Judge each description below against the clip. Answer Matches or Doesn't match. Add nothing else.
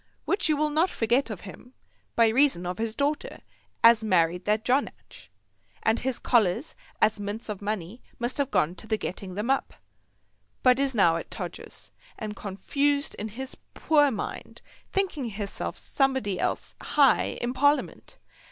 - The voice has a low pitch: Doesn't match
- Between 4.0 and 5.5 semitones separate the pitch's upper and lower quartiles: Matches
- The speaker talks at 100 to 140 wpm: Doesn't match